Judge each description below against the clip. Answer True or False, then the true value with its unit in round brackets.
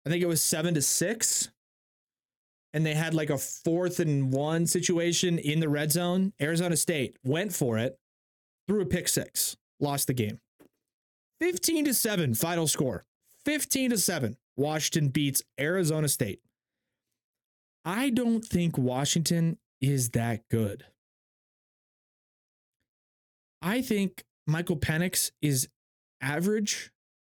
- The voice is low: False (160 Hz)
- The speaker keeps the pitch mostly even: False (4.9 semitones)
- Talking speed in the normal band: False (125 wpm)